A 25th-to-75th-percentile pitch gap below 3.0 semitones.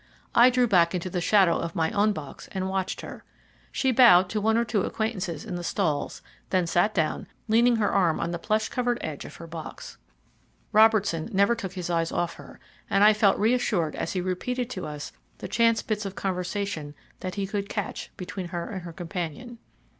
No: average, 4.1 semitones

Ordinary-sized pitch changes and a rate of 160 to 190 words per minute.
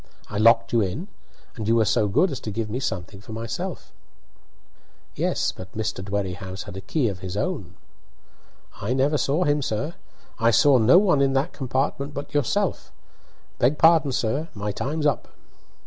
No: wide, 5.9 semitones; average, 175 wpm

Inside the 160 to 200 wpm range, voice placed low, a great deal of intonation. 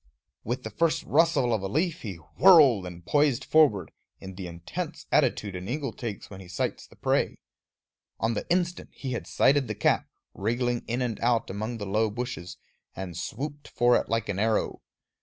Yes: average, 185 wpm; low, 115 Hz; wide, 5.9 semitones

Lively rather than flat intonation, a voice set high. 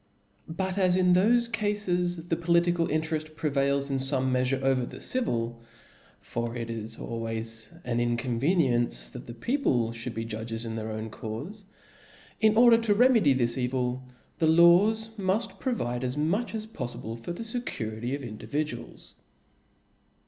No: wide, 7.9 semitones; medium, 140 Hz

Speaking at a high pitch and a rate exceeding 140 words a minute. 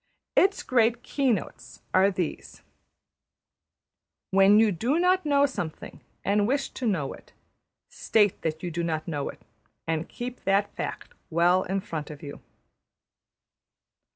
No: high, 195 Hz; slow, 135 wpm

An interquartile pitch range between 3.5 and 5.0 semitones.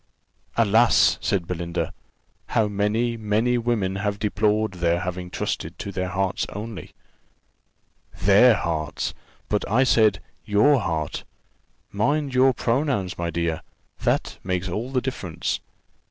Yes: average, 4.3 semitones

